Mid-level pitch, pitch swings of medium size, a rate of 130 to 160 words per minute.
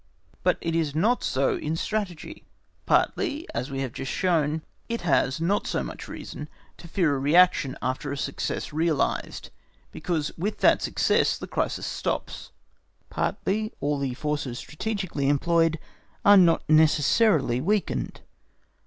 Yes: medium, 160 Hz; average, 4.5 semitones; average, 140 wpm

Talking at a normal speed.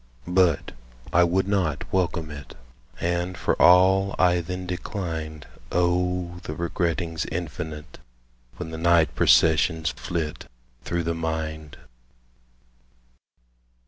No: slow, 105 wpm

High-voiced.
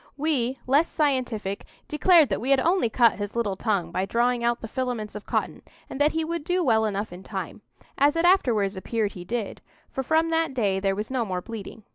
Yes: high, 235 Hz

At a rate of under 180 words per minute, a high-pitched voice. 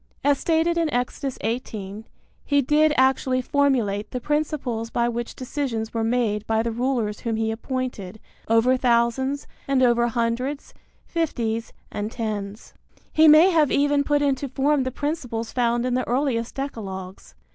Yes: average, 150 wpm; very high, 250 Hz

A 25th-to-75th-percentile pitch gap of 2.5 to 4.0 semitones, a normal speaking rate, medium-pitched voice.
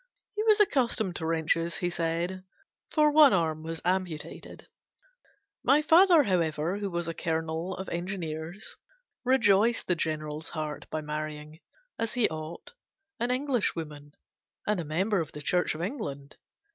No: wide, 5.4 semitones; average, 145 wpm; medium, 170 Hz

